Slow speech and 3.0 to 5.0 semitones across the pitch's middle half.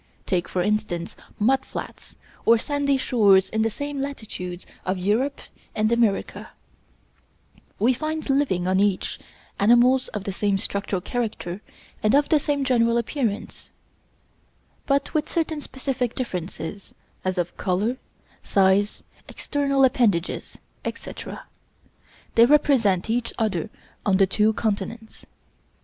No: slow, 125 wpm; wide, 5.4 semitones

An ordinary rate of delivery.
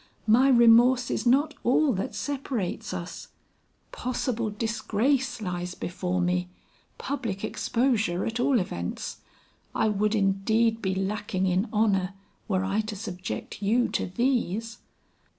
No: slow, 125 wpm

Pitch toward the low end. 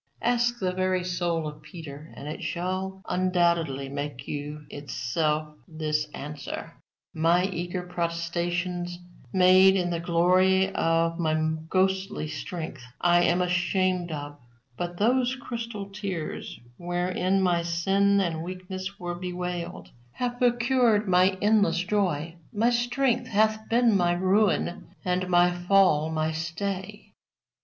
No: medium, 180 Hz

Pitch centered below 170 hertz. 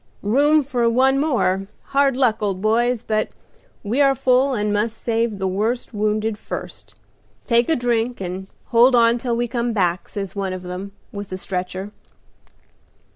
No: high, 225 Hz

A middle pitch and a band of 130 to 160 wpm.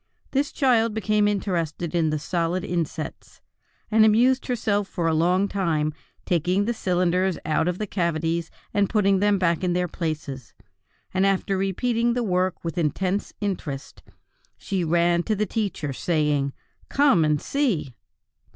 Yes: medium, 180 Hz; average, 150 wpm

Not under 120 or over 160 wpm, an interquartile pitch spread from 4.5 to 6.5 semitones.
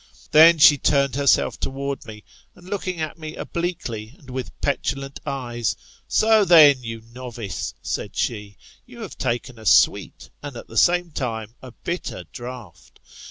Yes: average, 155 wpm; average, 5.2 semitones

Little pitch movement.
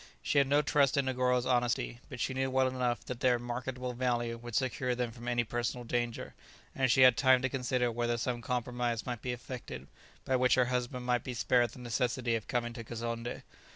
Yes: narrow, 1.3 semitones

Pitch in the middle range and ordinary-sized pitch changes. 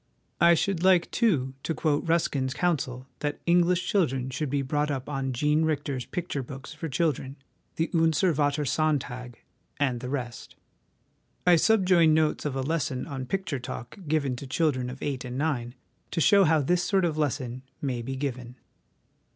Yes: medium, 145 Hz; average, 4.1 semitones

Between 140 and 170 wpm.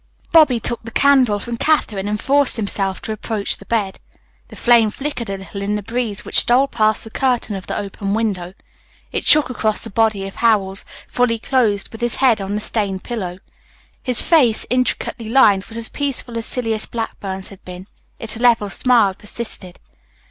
No: average, 185 wpm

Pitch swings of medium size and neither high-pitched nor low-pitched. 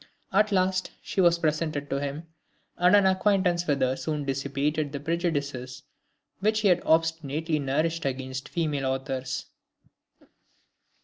Yes: average, 4.0 semitones; medium, 155 Hz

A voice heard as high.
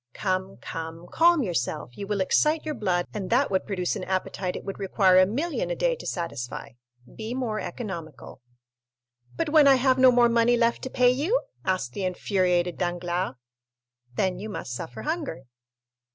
Yes: high, 200 Hz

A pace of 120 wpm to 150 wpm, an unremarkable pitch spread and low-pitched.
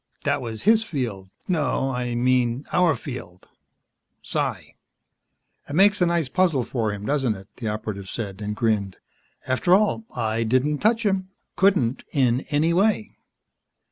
No: average, 145 wpm; wide, 7.9 semitones; low, 130 Hz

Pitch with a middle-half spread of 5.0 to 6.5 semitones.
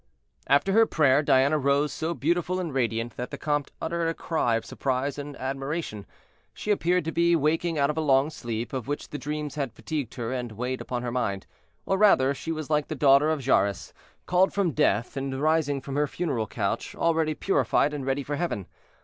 No: average, 3.6 semitones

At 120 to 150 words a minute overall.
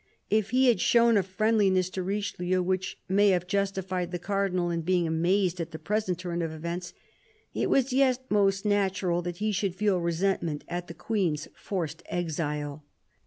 No: average, 170 wpm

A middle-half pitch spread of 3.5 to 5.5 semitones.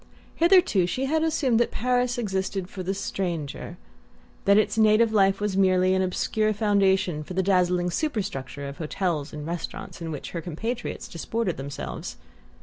Yes: average, 4.0 semitones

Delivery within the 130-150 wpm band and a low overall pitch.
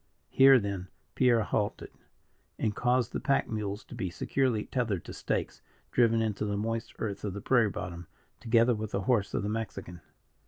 No: average, 180 wpm; low, 110 Hz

